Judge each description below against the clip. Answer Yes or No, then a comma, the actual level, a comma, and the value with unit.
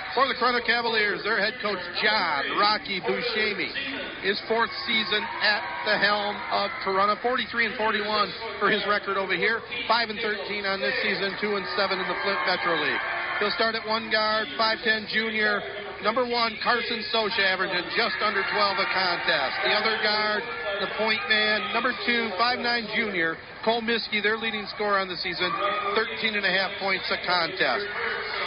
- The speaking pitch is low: No, high, 215 Hz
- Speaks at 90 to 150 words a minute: No, average, 175 wpm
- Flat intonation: Yes, narrow, 2.1 semitones